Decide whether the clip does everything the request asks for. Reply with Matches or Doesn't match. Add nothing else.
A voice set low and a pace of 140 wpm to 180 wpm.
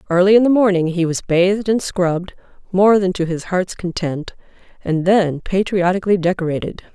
Doesn't match